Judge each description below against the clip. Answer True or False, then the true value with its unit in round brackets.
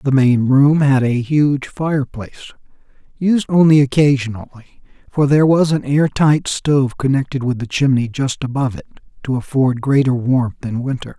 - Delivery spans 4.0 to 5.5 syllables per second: True (5.2 syllables/s)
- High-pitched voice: False (135 Hz)